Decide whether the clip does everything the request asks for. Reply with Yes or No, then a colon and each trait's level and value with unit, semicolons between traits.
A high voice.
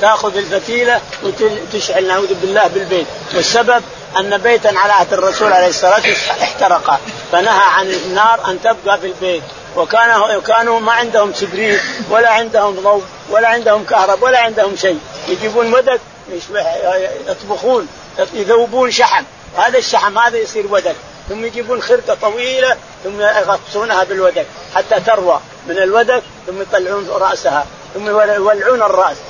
Yes: high, 210 Hz